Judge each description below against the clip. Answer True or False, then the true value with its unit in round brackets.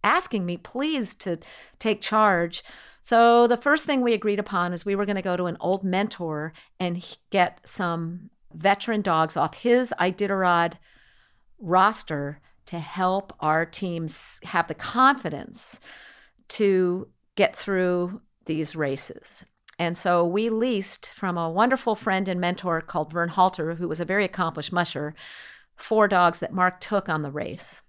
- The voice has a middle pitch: True (180 Hz)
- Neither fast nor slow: True (155 wpm)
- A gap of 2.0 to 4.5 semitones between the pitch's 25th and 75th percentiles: True (3.7 semitones)